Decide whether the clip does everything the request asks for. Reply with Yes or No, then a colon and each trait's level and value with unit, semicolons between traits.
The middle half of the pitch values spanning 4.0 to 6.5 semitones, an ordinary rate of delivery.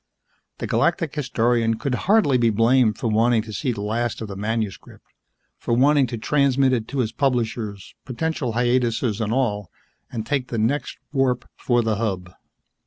No: average, 2.8 semitones; average, 170 wpm